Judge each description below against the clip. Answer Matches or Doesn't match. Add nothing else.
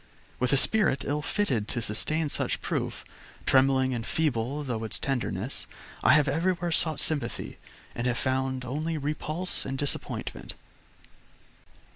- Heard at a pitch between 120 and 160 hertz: Matches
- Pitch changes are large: Doesn't match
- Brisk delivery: Doesn't match